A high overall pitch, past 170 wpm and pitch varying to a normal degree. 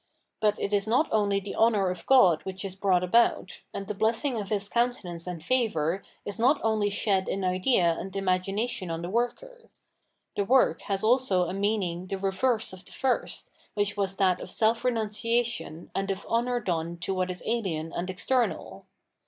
Yes: high, 200 Hz; average, 185 wpm; average, 3.9 semitones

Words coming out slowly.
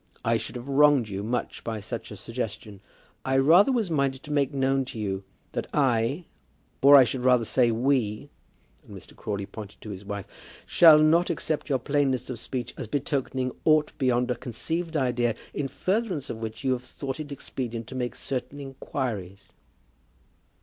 No: average, 175 wpm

